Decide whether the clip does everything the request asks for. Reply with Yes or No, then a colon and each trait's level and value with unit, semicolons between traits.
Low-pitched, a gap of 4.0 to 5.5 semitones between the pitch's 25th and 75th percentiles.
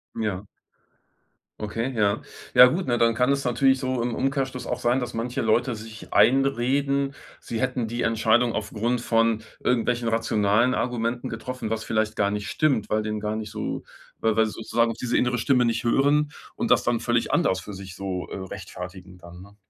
No: low, 115 Hz; average, 2.7 semitones